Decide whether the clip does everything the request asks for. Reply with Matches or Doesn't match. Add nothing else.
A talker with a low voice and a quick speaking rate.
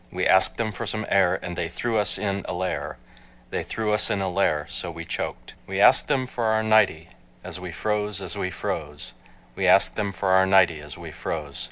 Matches